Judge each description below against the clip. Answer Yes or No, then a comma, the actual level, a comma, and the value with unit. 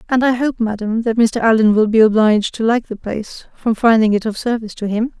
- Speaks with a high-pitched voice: Yes, high, 225 Hz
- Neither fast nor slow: No, fast, 240 wpm